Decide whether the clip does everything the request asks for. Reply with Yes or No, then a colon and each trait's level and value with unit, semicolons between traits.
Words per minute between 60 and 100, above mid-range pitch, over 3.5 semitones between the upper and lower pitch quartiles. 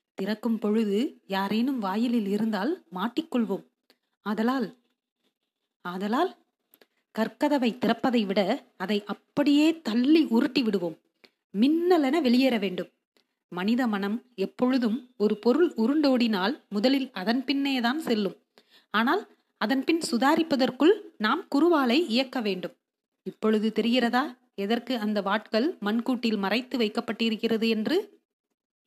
Yes: average, 95 wpm; high, 235 Hz; average, 4.2 semitones